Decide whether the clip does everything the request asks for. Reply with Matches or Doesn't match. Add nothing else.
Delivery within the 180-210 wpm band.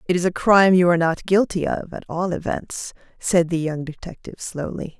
Matches